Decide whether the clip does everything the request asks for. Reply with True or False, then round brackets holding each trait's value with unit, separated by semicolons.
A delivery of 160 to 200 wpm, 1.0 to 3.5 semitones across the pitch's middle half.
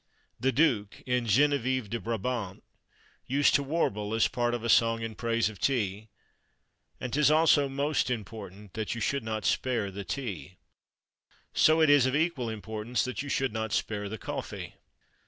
False (170 wpm; 3.9 semitones)